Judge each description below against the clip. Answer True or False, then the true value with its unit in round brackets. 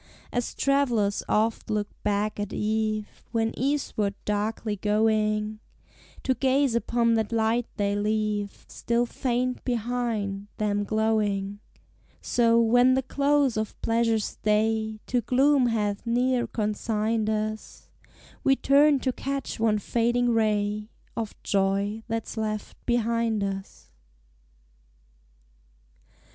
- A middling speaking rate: False (110 wpm)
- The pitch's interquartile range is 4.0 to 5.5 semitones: False (2.4 semitones)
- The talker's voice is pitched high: True (220 Hz)